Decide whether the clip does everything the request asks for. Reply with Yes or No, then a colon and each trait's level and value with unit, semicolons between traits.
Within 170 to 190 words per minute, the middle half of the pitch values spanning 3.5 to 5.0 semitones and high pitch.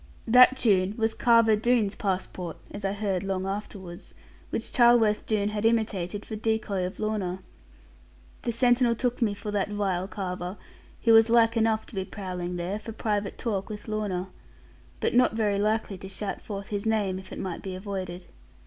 No: average, 175 wpm; average, 2.8 semitones; high, 205 Hz